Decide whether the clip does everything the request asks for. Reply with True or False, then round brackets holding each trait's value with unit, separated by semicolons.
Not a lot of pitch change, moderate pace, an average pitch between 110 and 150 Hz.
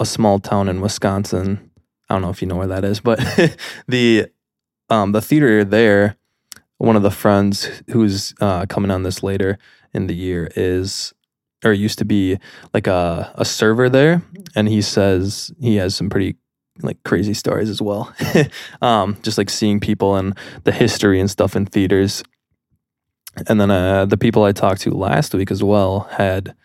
False (2.0 semitones; 180 wpm; 100 Hz)